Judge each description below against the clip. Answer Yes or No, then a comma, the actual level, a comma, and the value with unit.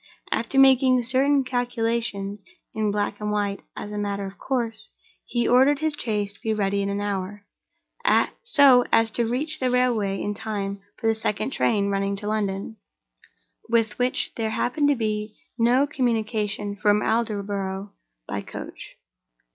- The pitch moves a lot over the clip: No, average, 3.4 semitones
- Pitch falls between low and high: No, high, 220 Hz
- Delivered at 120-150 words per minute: Yes, average, 145 wpm